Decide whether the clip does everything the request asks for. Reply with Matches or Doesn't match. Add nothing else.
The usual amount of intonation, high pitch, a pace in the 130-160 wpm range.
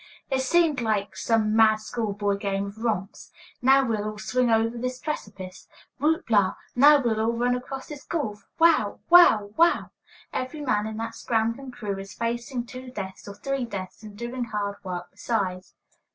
Doesn't match